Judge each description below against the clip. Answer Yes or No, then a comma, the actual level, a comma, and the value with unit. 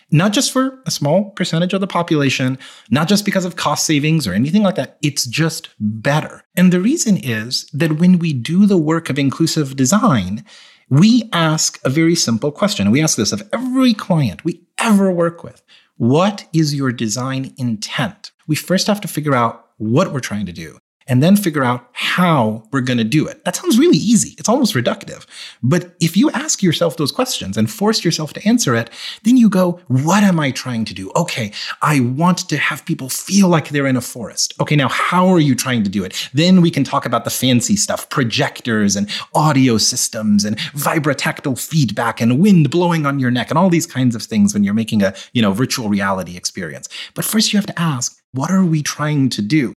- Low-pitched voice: No, medium, 155 Hz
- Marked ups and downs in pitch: Yes, wide, 6.3 semitones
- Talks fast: Yes, fast, 210 wpm